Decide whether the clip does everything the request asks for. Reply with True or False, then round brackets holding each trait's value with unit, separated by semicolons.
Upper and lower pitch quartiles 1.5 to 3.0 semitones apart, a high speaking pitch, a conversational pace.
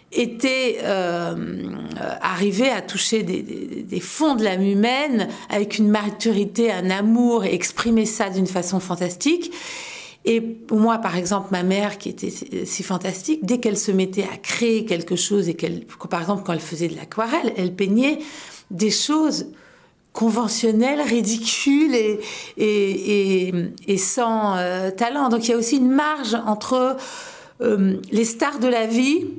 False (4.1 semitones; 220 Hz; 160 wpm)